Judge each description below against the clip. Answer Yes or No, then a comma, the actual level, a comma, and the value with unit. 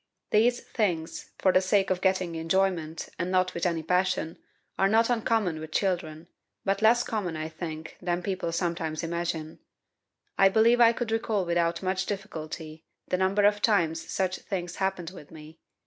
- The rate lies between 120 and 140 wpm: No, average, 165 wpm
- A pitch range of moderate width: Yes, average, 3.2 semitones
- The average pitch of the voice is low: No, medium, 185 Hz